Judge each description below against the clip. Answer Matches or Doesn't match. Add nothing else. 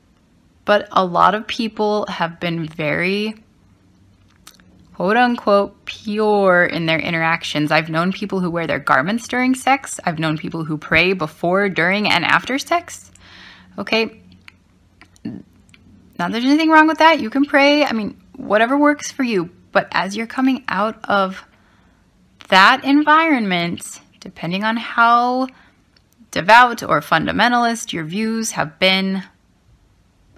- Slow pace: Matches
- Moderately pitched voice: Doesn't match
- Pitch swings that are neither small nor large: Doesn't match